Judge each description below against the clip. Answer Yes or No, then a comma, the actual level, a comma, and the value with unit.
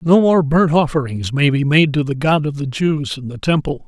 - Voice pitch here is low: No, medium, 150 Hz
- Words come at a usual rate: No, fast, 250 wpm